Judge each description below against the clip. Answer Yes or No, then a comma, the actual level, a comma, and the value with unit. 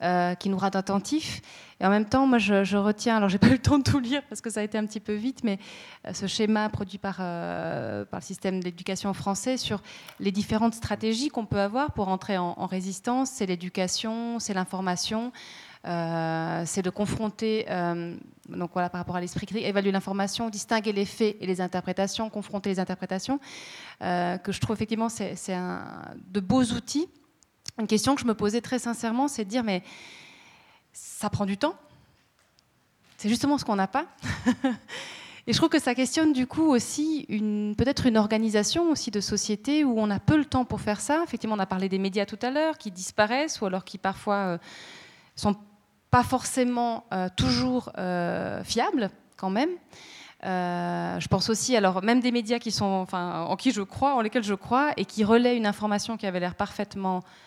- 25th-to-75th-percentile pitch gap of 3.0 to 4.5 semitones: Yes, average, 4.0 semitones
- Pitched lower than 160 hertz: No, high, 210 Hz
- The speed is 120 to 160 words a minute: No, average, 205 wpm